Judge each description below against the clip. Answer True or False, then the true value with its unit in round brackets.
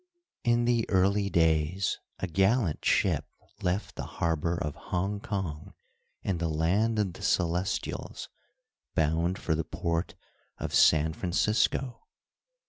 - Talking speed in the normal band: False (125 wpm)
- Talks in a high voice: False (90 Hz)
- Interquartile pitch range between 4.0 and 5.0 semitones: False (3.6 semitones)